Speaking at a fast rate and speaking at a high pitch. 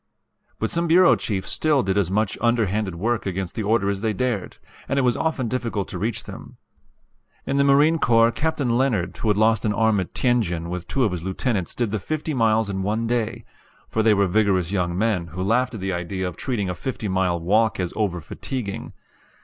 No: fast, 215 wpm; low, 110 Hz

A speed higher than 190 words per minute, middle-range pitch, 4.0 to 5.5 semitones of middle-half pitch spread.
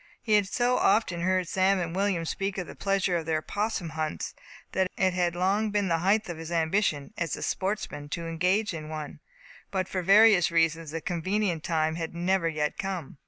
No: average, 200 wpm; medium, 180 Hz; average, 3.1 semitones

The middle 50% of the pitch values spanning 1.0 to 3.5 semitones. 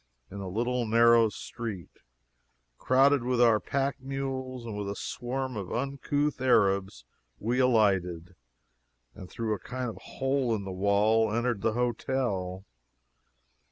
No: average, 4.3 semitones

